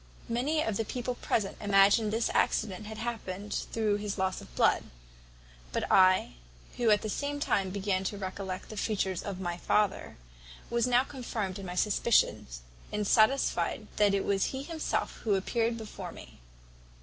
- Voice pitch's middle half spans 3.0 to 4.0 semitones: Yes, average, 3.3 semitones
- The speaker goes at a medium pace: Yes, average, 165 wpm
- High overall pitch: Yes, high, 210 Hz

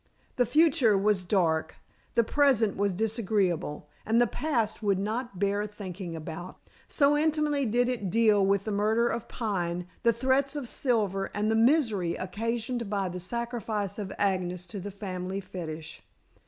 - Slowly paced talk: No, average, 155 wpm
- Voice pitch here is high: Yes, high, 210 Hz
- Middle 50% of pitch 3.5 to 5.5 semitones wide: Yes, average, 3.9 semitones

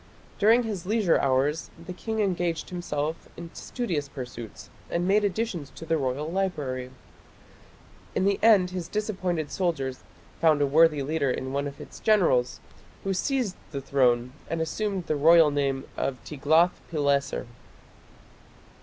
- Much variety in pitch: No, average, 5.0 semitones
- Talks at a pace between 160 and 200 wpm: No, average, 145 wpm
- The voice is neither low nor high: Yes, medium, 165 Hz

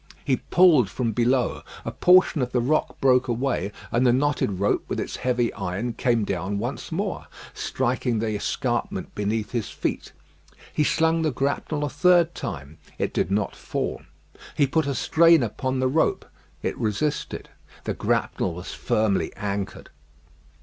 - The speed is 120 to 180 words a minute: Yes, average, 155 wpm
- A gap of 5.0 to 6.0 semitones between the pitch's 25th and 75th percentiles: Yes, wide, 5.5 semitones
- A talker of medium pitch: No, low, 125 Hz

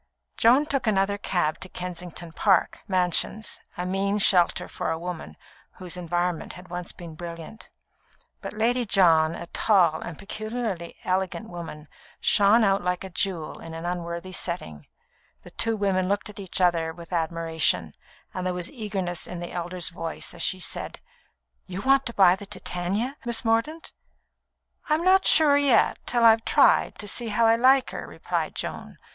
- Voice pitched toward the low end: No, medium, 185 Hz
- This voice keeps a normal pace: Yes, average, 165 wpm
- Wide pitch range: No, average, 4.2 semitones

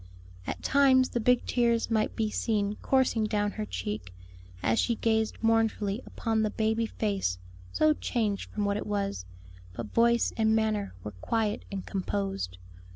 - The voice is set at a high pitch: Yes, high, 215 Hz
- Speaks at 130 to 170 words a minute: Yes, average, 155 wpm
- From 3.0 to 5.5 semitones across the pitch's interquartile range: No, narrow, 2.4 semitones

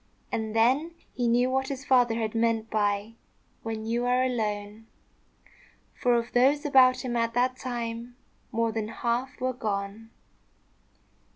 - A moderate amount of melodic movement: No, narrow, 2.3 semitones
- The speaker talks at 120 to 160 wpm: Yes, average, 145 wpm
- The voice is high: Yes, high, 235 Hz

